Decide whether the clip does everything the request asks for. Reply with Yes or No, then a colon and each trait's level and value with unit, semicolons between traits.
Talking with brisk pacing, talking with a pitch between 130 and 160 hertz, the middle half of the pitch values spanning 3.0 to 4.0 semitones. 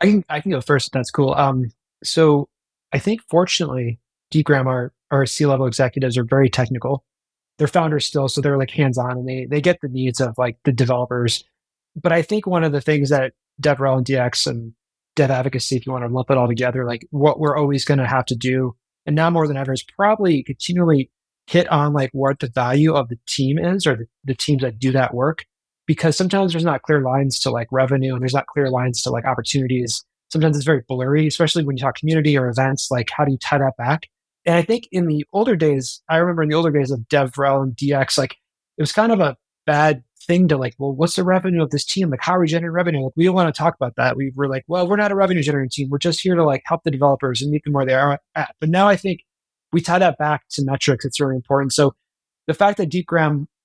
Yes: fast, 250 wpm; medium, 140 Hz; average, 3.7 semitones